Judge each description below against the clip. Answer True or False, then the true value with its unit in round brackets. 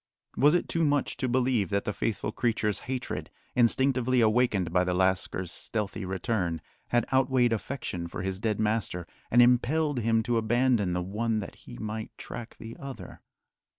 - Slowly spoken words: False (165 wpm)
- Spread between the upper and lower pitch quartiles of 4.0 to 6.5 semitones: True (4.3 semitones)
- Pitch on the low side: True (115 Hz)